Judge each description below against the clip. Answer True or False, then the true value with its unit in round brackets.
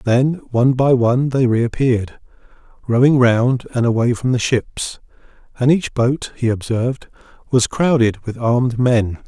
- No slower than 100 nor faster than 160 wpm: True (150 wpm)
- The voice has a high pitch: False (125 Hz)